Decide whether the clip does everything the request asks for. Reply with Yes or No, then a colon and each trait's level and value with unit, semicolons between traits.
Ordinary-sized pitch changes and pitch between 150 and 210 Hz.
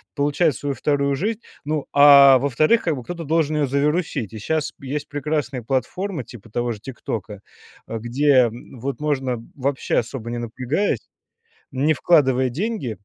No: average, 3.7 semitones; medium, 140 Hz